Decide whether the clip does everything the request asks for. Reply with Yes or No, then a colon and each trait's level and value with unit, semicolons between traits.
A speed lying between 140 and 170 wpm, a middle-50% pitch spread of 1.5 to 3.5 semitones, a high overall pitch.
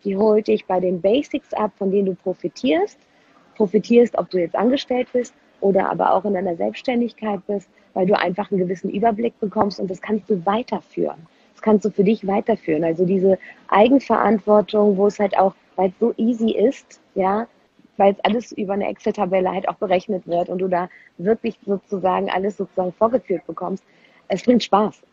No: average, 185 wpm; narrow, 2.6 semitones; high, 205 Hz